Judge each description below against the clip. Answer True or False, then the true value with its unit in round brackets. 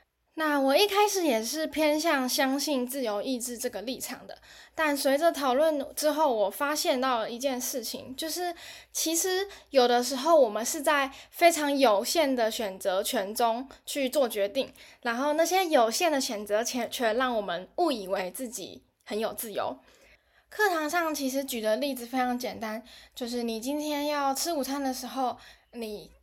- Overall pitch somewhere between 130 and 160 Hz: False (270 Hz)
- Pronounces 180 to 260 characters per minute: True (250 characters per minute)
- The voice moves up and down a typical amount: True (4.5 semitones)